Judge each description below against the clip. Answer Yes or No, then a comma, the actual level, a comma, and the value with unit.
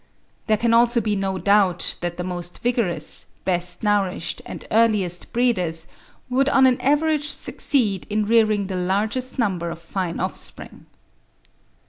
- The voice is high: Yes, high, 205 Hz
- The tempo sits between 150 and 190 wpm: No, average, 140 wpm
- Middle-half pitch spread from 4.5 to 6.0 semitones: Yes, average, 4.8 semitones